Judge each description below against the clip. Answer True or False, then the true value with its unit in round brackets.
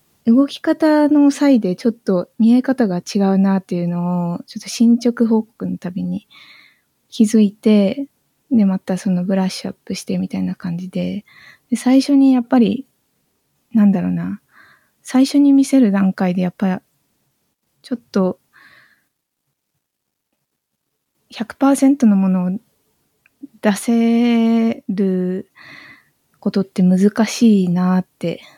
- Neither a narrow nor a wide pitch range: True (4.6 semitones)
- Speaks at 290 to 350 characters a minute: False (225 characters per minute)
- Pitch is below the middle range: False (210 Hz)